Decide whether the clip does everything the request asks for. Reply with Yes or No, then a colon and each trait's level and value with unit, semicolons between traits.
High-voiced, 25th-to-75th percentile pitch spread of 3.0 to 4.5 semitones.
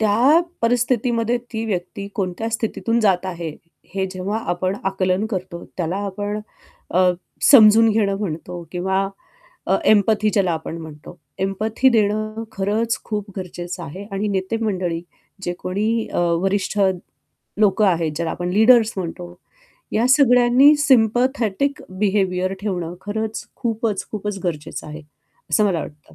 Yes: high, 205 Hz; average, 3.4 semitones